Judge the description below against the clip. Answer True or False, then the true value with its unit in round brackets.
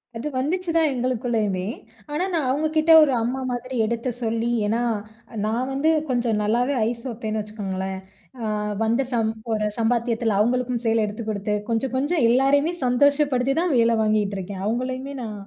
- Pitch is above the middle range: True (240 Hz)